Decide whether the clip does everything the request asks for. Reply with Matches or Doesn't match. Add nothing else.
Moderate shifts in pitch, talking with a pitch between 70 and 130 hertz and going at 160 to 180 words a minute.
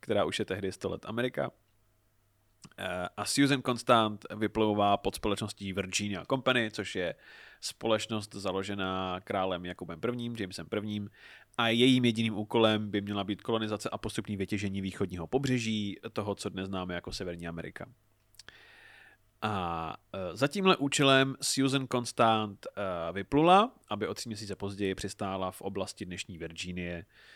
Doesn't match